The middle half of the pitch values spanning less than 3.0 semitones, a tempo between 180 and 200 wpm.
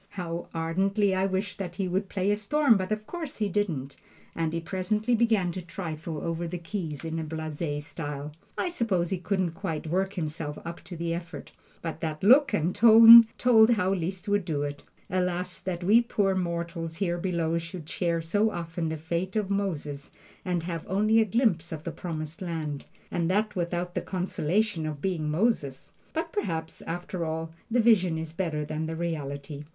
No: average, 3.5 semitones; average, 190 wpm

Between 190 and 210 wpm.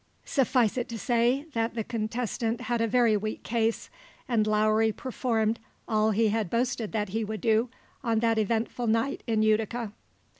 No: average, 165 wpm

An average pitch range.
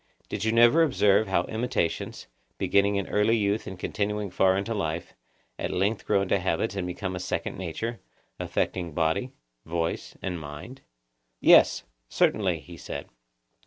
Yes: average, 3.6 semitones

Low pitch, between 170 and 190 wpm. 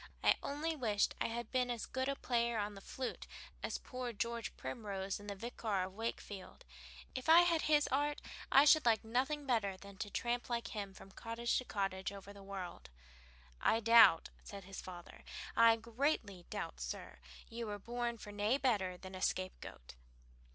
No: high, 225 Hz; average, 180 wpm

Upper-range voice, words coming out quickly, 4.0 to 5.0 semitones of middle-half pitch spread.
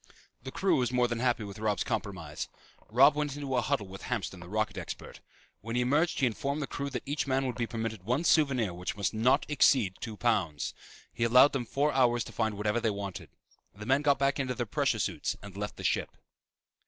No: low, 120 Hz; fast, 220 wpm; average, 4.3 semitones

